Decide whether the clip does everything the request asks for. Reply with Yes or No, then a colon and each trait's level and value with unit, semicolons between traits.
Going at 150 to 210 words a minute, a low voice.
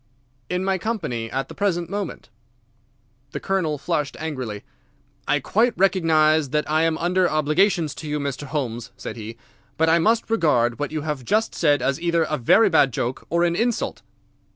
No: average, 175 wpm; medium, 155 Hz